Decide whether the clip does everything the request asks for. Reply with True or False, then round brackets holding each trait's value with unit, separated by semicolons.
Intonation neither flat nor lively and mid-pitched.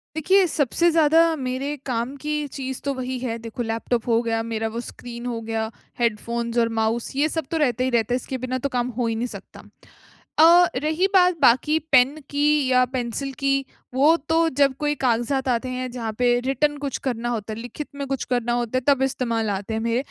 False (3.3 semitones; 255 Hz)